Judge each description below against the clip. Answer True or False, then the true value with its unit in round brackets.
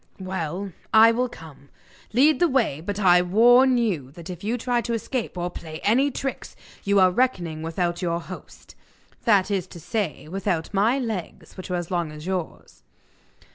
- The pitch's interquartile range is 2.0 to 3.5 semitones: False (5.1 semitones)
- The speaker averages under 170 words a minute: False (175 wpm)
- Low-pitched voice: False (190 Hz)